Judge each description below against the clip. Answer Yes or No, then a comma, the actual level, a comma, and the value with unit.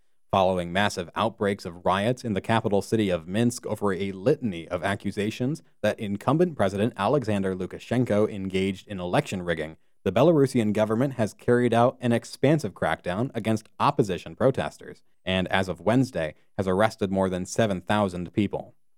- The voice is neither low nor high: No, low, 105 Hz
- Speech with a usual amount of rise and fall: Yes, average, 3.5 semitones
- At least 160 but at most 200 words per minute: No, average, 150 wpm